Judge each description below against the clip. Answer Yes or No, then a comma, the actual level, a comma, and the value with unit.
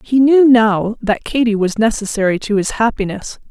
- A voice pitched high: Yes, high, 220 Hz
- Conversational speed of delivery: Yes, average, 170 wpm